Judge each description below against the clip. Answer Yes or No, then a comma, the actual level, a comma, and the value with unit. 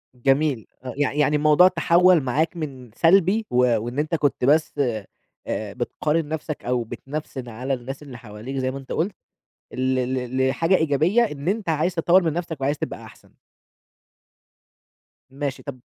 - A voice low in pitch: No, medium, 145 Hz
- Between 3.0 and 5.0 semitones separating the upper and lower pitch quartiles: Yes, average, 4.1 semitones